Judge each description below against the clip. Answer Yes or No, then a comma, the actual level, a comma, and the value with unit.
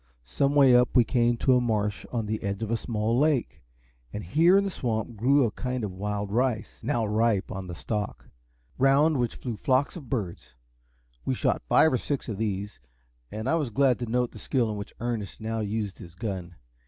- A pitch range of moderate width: Yes, average, 3.7 semitones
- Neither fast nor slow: No, fast, 210 wpm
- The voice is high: No, low, 115 Hz